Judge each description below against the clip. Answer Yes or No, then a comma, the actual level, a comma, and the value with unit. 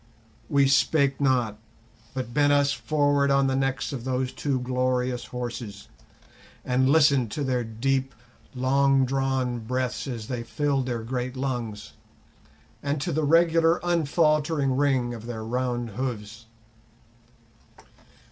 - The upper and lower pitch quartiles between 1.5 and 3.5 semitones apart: Yes, narrow, 2.4 semitones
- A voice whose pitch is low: Yes, low, 130 Hz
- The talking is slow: Yes, slow, 130 wpm